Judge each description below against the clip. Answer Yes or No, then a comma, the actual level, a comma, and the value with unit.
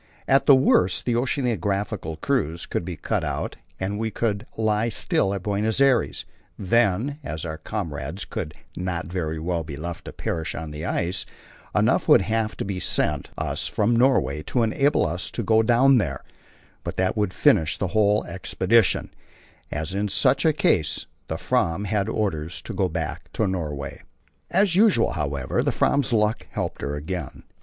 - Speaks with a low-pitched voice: Yes, very low, 95 Hz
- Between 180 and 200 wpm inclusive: No, average, 170 wpm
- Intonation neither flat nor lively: No, wide, 5.7 semitones